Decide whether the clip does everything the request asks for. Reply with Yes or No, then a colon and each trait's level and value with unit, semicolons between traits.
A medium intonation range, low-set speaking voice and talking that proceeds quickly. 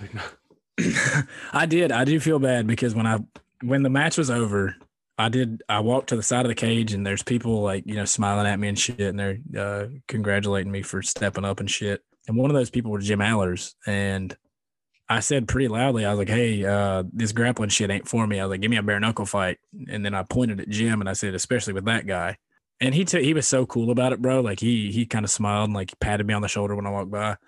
Yes: average, 3.5 semitones; low, 110 Hz; fast, 260 wpm